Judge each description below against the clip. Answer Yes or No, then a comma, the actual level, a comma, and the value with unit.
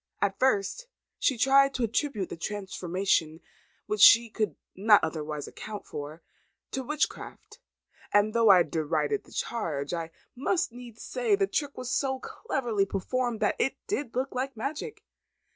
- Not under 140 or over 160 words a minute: Yes, average, 150 wpm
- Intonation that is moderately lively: No, wide, 5.9 semitones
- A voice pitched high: Yes, high, 230 Hz